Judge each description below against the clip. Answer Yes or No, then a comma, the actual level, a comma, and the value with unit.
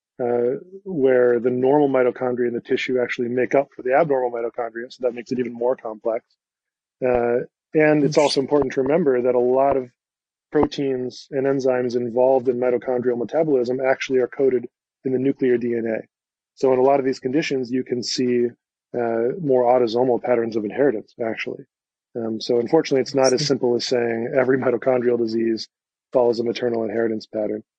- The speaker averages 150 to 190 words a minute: Yes, average, 175 wpm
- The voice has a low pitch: Yes, low, 125 Hz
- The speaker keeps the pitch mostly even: Yes, narrow, 1.8 semitones